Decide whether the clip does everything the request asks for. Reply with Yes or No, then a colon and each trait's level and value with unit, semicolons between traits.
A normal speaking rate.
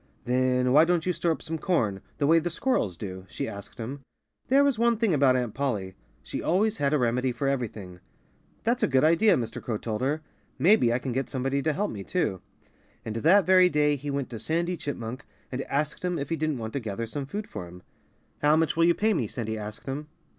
No: fast, 230 wpm